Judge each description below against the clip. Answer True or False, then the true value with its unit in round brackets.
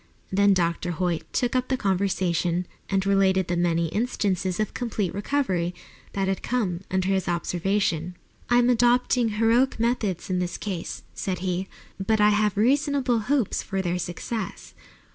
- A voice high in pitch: True (195 Hz)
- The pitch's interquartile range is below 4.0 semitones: False (4.3 semitones)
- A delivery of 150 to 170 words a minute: True (155 wpm)